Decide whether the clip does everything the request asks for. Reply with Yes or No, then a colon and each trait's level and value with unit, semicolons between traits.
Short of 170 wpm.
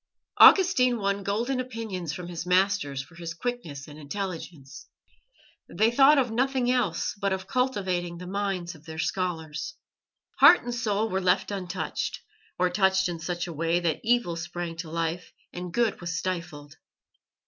Yes: average, 160 wpm